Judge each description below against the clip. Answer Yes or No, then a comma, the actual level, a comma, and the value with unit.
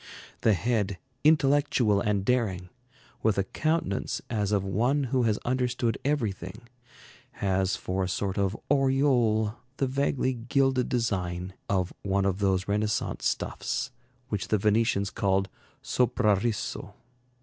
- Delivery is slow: Yes, slow, 125 wpm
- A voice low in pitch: Yes, low, 105 Hz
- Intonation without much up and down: No, average, 4.4 semitones